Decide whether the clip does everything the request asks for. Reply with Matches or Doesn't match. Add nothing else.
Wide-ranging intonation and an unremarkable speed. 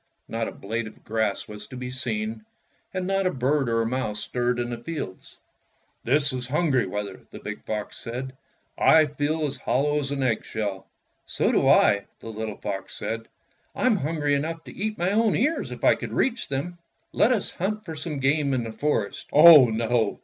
Matches